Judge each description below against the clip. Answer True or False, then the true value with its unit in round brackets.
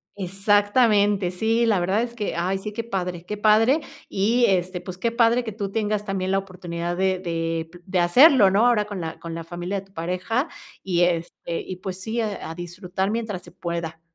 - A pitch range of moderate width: True (3.4 semitones)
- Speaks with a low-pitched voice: False (195 Hz)